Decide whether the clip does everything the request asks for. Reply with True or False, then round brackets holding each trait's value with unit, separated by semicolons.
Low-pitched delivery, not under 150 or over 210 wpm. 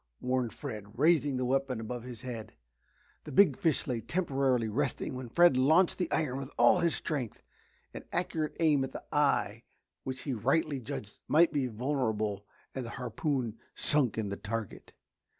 True (130 Hz; 170 wpm)